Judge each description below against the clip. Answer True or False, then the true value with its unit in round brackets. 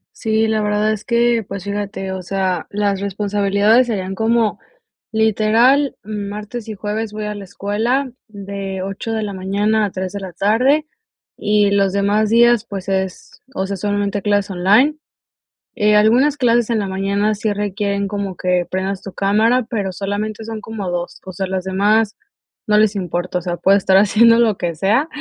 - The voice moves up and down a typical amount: False (2.1 semitones)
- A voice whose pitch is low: False (205 Hz)